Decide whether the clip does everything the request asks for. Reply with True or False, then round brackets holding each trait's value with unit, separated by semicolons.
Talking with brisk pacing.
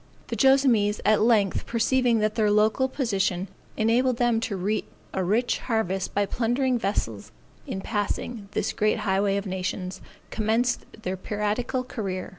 False (145 wpm)